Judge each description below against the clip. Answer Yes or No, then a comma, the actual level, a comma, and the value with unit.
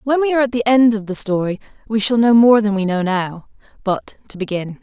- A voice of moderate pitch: No, high, 215 Hz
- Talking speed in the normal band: No, fast, 250 wpm